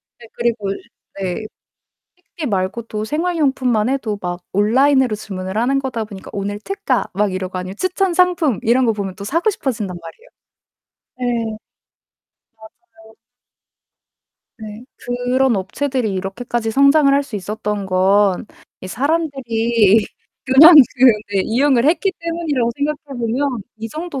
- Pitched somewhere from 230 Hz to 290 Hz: Yes, high, 235 Hz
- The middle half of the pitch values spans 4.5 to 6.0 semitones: Yes, average, 5.2 semitones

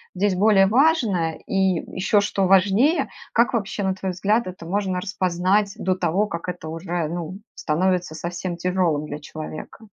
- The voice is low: No, medium, 185 Hz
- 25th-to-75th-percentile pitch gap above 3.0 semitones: No, average, 2.7 semitones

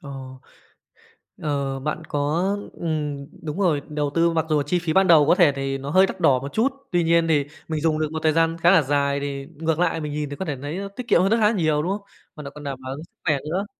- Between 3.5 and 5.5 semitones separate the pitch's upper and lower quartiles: No, average, 3.0 semitones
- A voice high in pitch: No, medium, 155 Hz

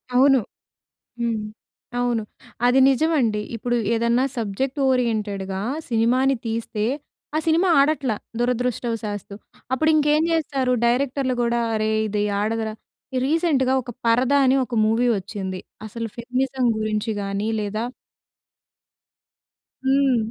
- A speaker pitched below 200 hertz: No, high, 240 Hz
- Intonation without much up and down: No, average, 3.5 semitones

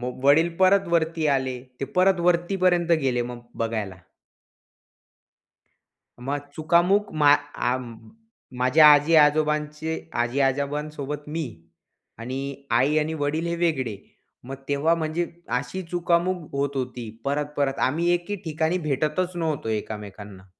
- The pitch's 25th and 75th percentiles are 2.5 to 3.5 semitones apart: No, average, 4.0 semitones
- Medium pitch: Yes, medium, 150 Hz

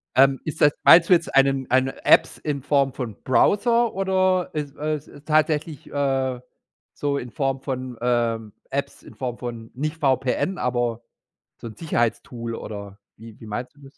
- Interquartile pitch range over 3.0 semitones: Yes, average, 3.8 semitones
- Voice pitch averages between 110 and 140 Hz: Yes, low, 135 Hz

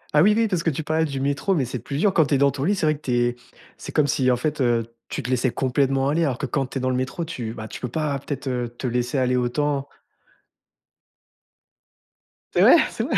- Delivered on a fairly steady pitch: No, average, 3.3 semitones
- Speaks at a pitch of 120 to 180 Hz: Yes, low, 135 Hz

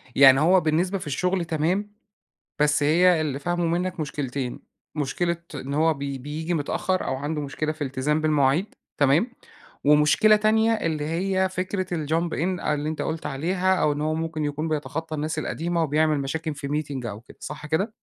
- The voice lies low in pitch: No, medium, 155 Hz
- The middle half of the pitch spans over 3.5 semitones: No, average, 3.1 semitones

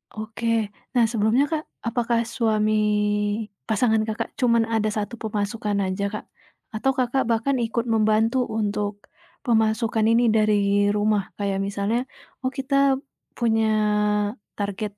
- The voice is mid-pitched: No, high, 220 Hz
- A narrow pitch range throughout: Yes, narrow, 1.9 semitones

